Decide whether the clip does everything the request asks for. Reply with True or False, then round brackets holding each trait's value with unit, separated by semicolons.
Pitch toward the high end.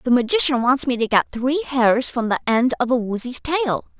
True (255 Hz)